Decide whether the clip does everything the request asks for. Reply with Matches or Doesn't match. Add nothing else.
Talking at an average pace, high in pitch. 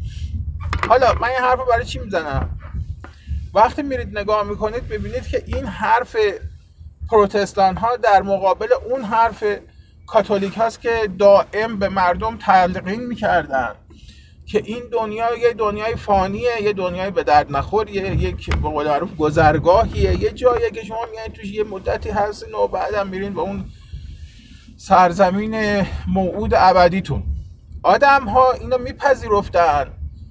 Matches